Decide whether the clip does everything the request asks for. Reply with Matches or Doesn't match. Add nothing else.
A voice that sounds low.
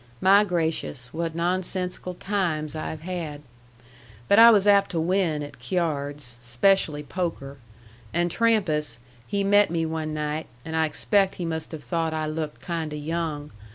Doesn't match